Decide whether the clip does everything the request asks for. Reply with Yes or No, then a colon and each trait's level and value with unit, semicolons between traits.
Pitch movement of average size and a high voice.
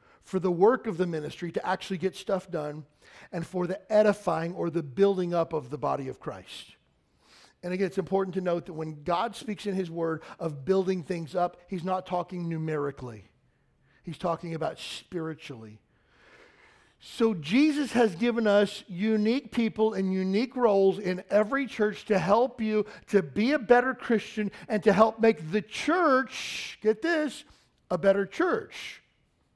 Yes: average, 4.1 semitones; high, 195 Hz